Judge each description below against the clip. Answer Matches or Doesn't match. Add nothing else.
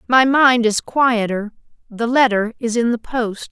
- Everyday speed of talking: Matches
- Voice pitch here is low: Doesn't match